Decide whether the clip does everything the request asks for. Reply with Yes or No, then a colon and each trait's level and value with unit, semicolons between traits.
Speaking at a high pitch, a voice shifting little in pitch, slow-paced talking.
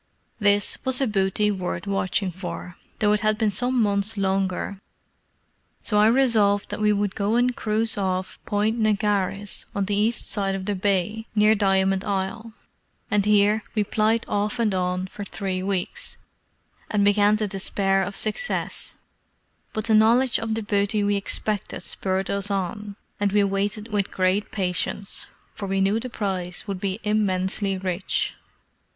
No: high, 205 Hz; narrow, 1.8 semitones; average, 160 wpm